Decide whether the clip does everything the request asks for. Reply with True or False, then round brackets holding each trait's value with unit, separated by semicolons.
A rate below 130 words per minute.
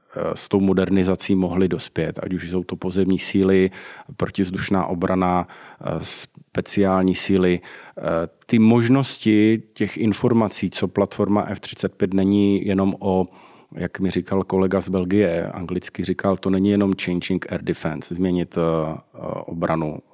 True (120 wpm)